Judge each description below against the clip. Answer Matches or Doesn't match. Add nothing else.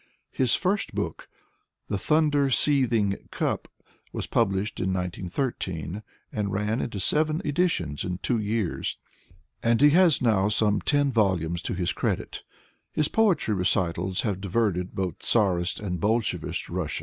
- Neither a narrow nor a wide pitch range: Doesn't match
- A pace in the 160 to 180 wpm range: Doesn't match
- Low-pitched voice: Matches